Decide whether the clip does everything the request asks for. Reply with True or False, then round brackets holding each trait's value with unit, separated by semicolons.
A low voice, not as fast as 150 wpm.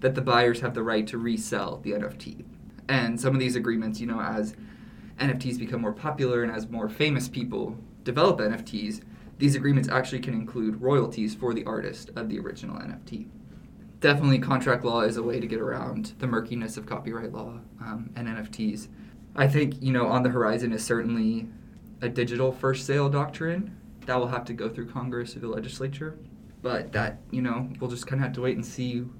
False (120 Hz; 195 wpm)